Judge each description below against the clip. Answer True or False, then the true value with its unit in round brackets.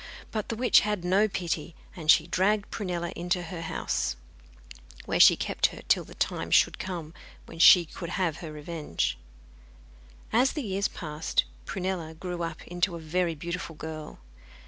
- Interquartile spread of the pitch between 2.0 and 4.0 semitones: True (2.7 semitones)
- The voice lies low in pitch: False (175 Hz)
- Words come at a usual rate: True (165 wpm)